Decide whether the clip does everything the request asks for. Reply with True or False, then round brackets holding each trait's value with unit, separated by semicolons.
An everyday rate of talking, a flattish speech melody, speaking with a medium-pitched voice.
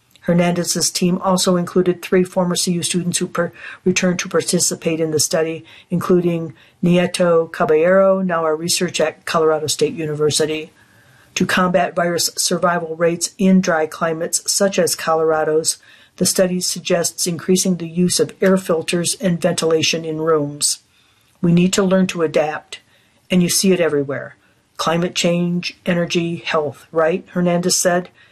True (145 wpm; 2.2 semitones; 175 Hz)